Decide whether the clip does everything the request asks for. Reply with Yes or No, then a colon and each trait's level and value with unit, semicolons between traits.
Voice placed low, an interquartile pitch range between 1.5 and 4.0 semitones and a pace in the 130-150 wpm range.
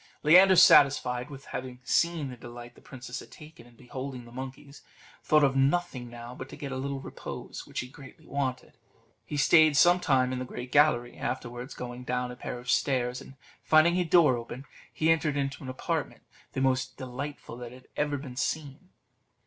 No: low, 130 Hz; average, 2.9 semitones; average, 190 wpm